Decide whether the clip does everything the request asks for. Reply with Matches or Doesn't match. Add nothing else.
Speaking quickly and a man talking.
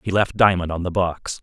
Matches